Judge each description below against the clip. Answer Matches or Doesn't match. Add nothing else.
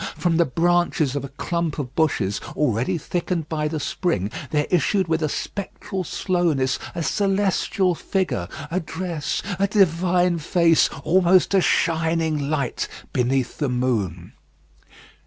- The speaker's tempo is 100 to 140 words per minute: Matches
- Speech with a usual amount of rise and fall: Matches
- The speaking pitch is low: Doesn't match